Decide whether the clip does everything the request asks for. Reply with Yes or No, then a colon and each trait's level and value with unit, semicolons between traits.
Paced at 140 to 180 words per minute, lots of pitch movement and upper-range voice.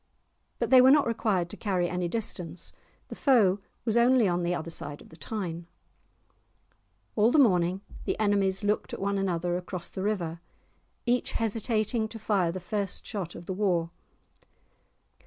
No: average, 165 wpm; average, 3.8 semitones; high, 195 Hz